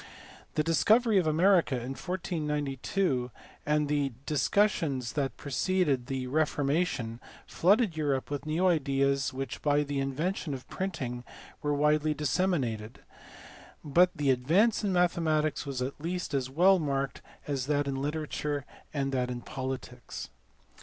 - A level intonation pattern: No, average, 3.7 semitones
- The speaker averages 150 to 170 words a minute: No, slow, 135 wpm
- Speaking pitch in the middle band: Yes, medium, 145 Hz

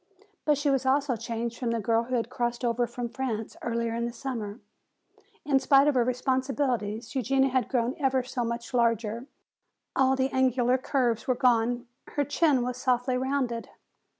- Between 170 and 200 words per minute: Yes, average, 175 wpm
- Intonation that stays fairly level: Yes, narrow, 2.2 semitones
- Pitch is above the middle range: Yes, very high, 250 Hz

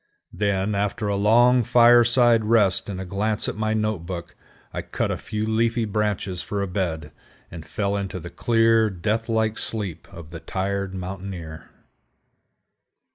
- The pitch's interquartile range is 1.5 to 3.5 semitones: Yes, average, 2.9 semitones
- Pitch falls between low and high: No, low, 100 Hz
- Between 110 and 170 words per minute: Yes, average, 155 wpm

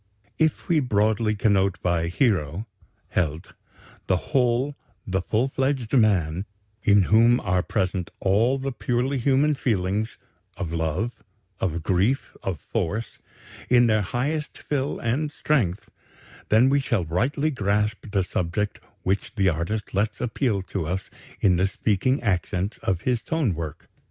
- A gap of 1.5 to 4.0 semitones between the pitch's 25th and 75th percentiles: No, average, 5.3 semitones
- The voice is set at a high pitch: No, low, 105 Hz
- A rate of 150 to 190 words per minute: No, average, 140 wpm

